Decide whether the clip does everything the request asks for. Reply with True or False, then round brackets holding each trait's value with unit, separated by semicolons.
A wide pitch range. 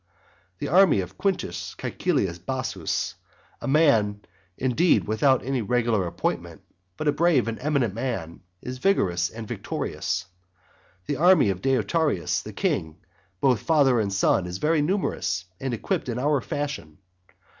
True (7.1 semitones)